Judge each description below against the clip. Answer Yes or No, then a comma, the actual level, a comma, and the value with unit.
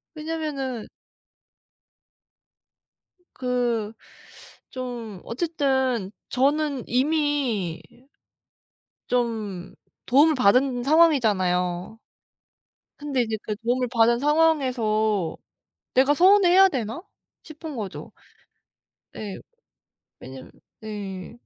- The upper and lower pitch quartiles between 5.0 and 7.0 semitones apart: Yes, wide, 5.4 semitones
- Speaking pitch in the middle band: No, very high, 250 Hz